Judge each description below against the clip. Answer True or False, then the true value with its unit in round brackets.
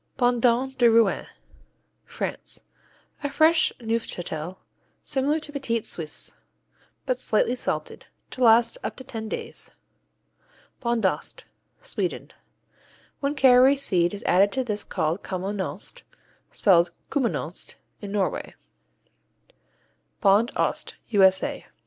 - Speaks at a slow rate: True (105 wpm)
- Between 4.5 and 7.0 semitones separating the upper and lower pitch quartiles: True (4.9 semitones)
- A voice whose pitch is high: True (230 Hz)